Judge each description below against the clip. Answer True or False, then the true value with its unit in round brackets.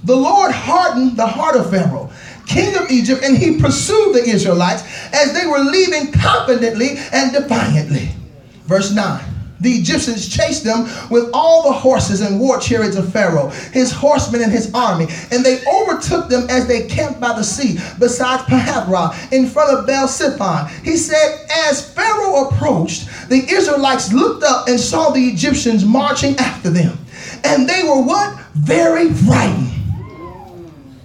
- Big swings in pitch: True (6.7 semitones)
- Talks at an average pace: True (155 wpm)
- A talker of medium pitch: False (250 Hz)